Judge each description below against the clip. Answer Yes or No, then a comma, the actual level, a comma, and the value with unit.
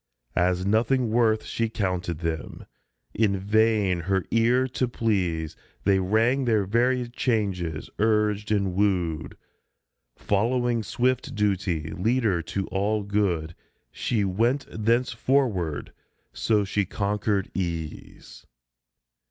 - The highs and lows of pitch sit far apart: No, average, 3.7 semitones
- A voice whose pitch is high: No, low, 105 Hz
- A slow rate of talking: Yes, slow, 105 wpm